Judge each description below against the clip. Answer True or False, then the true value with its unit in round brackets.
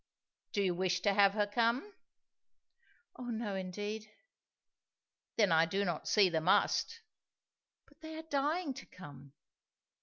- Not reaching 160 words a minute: True (140 wpm)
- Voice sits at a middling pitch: False (205 Hz)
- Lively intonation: True (6.0 semitones)